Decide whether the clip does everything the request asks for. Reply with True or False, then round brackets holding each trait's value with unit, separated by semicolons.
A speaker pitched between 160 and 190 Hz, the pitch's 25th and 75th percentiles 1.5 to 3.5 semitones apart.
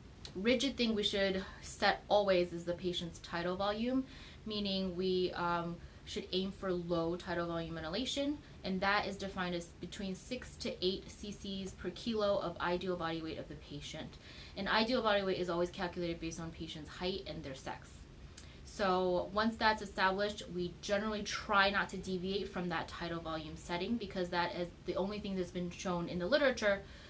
True (185 Hz; 2.7 semitones)